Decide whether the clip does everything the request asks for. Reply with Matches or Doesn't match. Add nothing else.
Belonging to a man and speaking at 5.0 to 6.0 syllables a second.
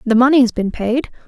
Doesn't match